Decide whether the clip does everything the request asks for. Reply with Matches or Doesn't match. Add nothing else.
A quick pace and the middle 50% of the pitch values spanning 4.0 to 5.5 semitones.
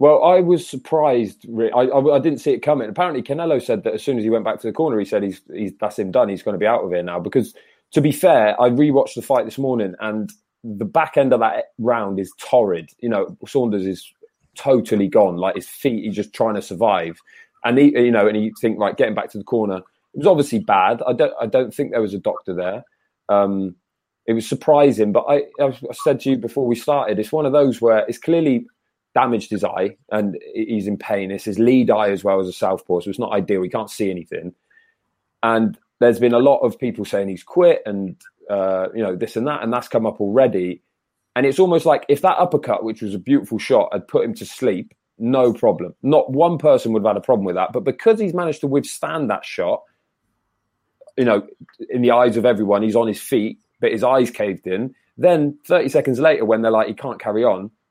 Matches